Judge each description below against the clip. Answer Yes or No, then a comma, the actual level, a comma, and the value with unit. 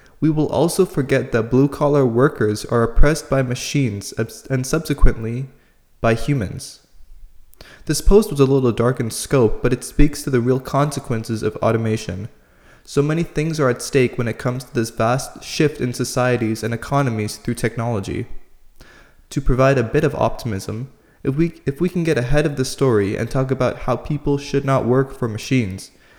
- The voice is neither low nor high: No, low, 130 Hz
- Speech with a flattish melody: No, average, 3.6 semitones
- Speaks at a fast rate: No, average, 180 wpm